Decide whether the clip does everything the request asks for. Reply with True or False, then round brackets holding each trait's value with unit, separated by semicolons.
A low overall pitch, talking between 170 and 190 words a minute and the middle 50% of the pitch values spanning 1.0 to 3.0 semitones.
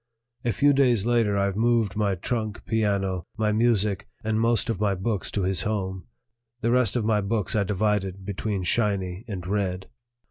True (105 Hz; 175 wpm; 2.7 semitones)